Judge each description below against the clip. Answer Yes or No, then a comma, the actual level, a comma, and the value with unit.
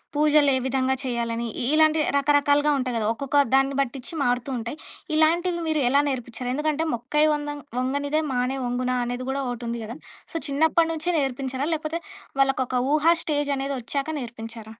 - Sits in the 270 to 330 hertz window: Yes, very high, 275 Hz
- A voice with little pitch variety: No, average, 3.3 semitones